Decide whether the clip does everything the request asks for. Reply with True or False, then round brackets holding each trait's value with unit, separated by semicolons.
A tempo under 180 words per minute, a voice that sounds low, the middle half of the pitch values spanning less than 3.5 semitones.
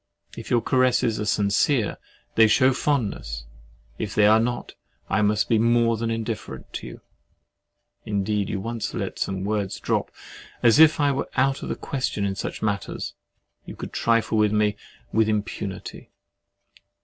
True (160 wpm; 110 Hz; 2.7 semitones)